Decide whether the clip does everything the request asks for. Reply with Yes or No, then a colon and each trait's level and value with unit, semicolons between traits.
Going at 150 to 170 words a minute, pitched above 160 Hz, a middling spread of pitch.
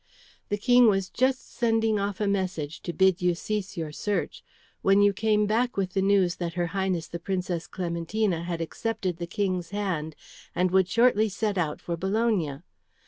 No: average, 180 wpm; high, 190 Hz; average, 3.4 semitones